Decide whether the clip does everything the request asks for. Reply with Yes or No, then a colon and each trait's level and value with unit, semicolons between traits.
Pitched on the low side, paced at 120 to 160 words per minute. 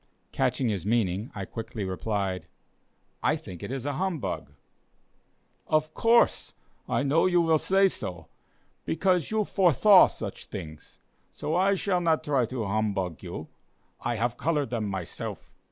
Yes: low, 125 Hz; average, 145 wpm